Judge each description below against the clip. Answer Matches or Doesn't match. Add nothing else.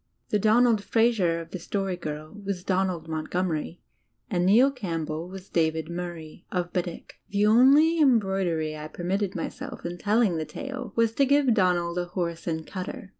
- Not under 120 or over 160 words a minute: Doesn't match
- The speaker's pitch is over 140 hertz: Matches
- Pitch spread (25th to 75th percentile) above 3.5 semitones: Matches